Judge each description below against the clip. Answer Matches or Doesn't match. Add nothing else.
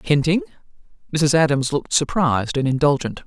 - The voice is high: Doesn't match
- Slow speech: Matches